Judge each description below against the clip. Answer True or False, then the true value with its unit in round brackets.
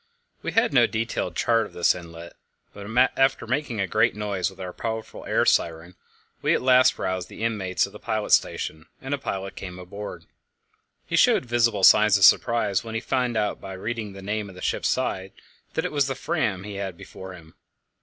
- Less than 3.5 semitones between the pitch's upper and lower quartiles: False (3.9 semitones)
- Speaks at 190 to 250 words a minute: True (205 wpm)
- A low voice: True (105 Hz)